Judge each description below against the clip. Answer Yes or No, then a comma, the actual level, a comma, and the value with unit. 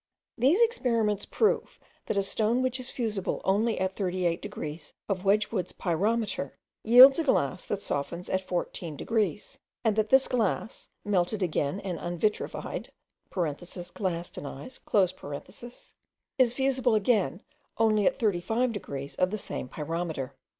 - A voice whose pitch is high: Yes, high, 205 Hz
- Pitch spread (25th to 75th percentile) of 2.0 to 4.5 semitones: No, average, 4.9 semitones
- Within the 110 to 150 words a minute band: Yes, slow, 135 wpm